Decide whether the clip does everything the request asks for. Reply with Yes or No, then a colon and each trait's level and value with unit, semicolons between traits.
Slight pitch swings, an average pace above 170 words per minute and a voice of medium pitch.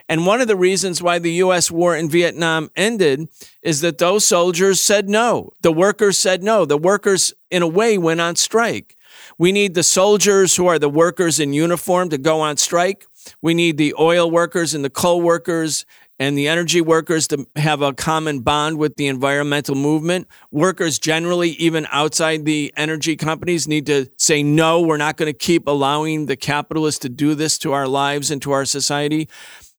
No: average, 3.0 semitones; average, 190 wpm; medium, 165 Hz